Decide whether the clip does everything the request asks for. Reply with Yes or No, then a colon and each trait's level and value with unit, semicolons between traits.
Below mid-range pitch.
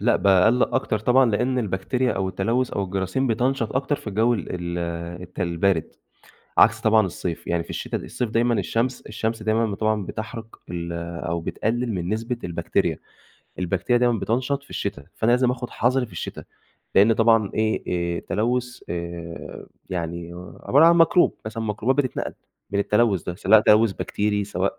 Yes: low, 110 Hz